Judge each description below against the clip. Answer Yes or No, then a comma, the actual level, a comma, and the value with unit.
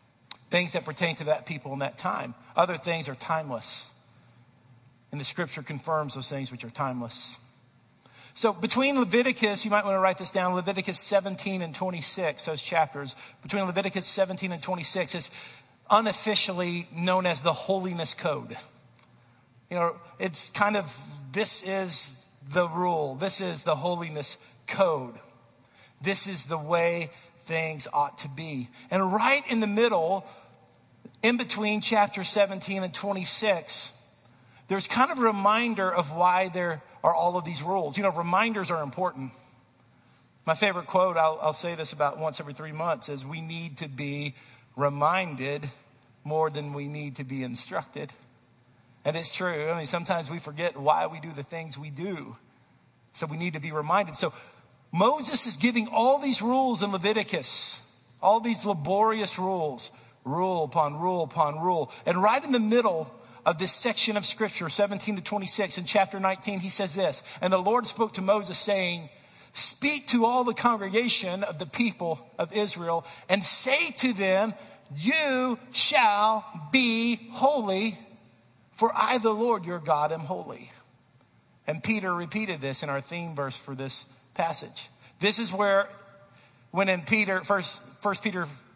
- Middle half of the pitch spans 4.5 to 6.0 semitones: Yes, wide, 5.6 semitones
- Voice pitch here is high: No, medium, 175 Hz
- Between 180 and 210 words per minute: No, average, 160 wpm